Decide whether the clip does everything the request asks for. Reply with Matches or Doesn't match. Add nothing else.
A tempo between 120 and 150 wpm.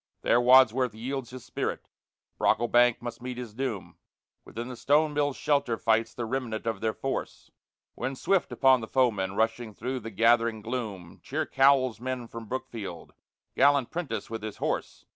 Doesn't match